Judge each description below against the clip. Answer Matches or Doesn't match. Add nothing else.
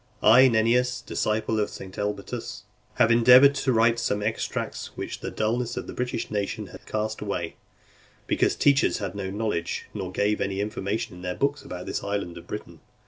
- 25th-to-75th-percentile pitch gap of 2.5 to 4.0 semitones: Matches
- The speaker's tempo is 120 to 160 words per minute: Doesn't match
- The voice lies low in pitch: Matches